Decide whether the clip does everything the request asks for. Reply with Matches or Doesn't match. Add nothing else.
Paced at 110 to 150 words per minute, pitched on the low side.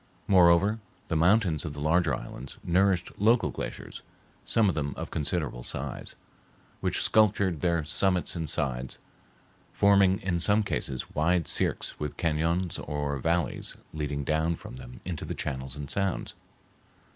Matches